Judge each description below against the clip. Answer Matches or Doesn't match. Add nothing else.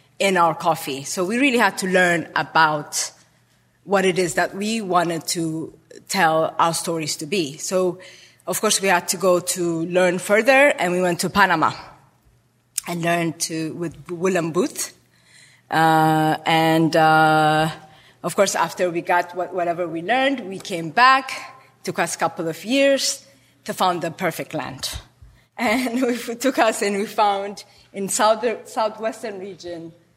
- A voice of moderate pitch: Matches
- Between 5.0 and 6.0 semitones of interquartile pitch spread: Doesn't match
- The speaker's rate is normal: Matches